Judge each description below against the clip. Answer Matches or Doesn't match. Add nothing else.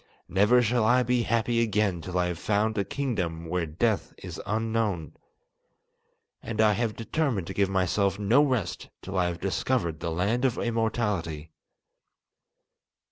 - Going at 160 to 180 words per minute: Doesn't match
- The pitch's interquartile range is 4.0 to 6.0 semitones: Matches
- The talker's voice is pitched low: Matches